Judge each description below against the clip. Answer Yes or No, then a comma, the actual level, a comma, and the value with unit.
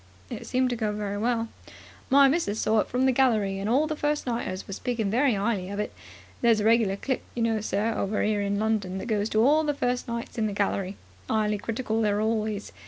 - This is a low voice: No, high, 220 Hz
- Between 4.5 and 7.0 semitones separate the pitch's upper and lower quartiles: No, average, 3.1 semitones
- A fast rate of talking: Yes, fast, 235 wpm